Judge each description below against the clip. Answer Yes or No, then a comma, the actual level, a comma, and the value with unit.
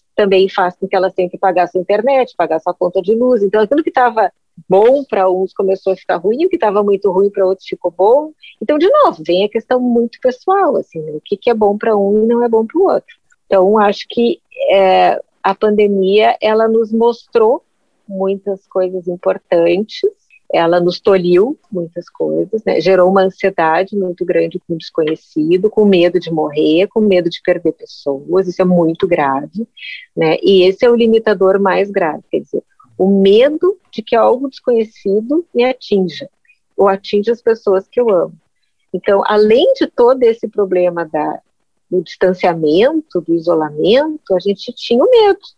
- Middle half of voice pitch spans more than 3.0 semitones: Yes, average, 4.4 semitones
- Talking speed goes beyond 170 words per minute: Yes, fast, 185 wpm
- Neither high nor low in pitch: No, high, 200 Hz